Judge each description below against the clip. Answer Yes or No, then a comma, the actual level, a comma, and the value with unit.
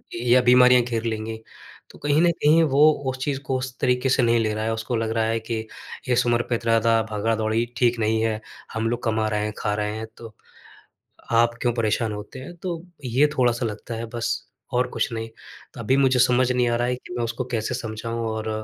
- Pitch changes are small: Yes, narrow, 2.0 semitones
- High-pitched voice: No, low, 115 Hz